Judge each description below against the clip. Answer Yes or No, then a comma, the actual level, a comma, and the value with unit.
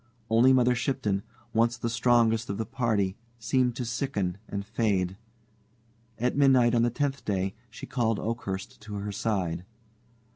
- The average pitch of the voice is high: No, low, 115 Hz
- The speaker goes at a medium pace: Yes, average, 150 wpm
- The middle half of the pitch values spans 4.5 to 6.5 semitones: No, average, 3.4 semitones